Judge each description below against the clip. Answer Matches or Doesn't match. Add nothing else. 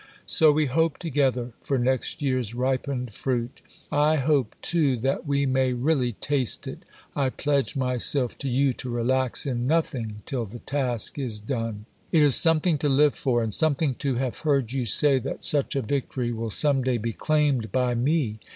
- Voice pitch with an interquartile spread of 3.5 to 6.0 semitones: Doesn't match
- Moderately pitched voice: Doesn't match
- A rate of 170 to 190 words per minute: Matches